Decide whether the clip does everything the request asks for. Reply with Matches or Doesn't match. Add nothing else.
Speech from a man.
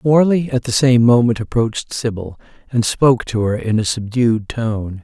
Matches